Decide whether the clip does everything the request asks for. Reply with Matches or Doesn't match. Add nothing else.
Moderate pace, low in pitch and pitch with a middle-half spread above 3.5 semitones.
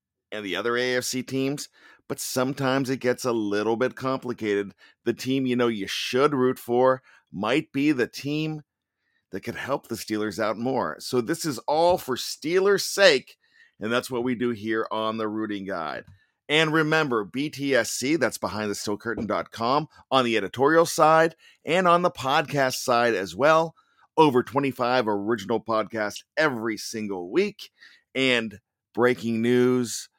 Matches